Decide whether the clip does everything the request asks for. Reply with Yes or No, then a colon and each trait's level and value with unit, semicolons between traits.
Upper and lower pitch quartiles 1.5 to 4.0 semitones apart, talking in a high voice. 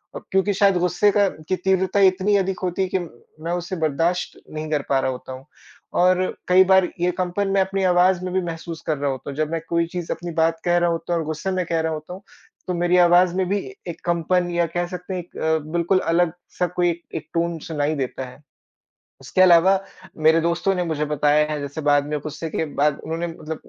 No: narrow, 2.5 semitones; medium, 175 Hz